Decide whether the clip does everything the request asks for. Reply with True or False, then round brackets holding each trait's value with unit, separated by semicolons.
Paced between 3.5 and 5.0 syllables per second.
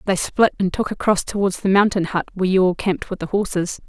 False (6.2 syllables/s)